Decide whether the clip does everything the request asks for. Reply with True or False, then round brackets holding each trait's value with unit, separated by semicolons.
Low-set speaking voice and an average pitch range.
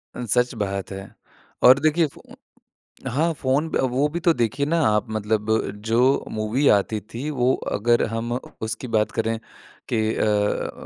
True (120 Hz; 4.0 semitones)